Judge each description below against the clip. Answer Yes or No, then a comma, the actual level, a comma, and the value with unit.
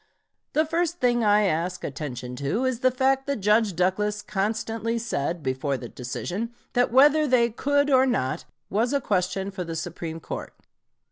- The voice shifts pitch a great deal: Yes, wide, 6.7 semitones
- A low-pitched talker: No, high, 210 Hz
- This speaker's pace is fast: No, average, 165 wpm